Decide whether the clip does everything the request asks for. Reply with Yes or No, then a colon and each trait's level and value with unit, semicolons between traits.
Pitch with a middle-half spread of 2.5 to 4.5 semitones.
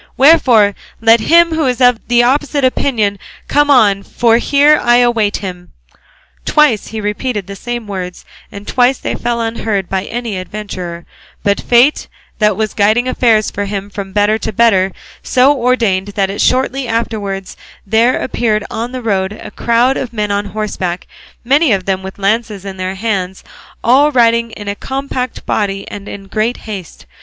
Yes: average, 3.6 semitones